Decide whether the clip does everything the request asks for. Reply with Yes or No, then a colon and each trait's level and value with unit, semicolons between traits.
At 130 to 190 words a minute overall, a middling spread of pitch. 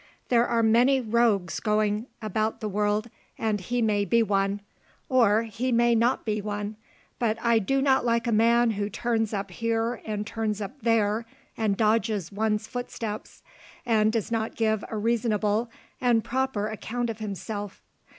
No: average, 160 wpm; narrow, 1.9 semitones